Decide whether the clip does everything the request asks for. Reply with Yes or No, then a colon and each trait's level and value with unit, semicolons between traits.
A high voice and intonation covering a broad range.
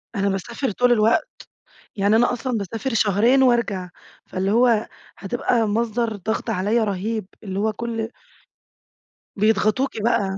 No: high, 220 Hz; average, 2.8 semitones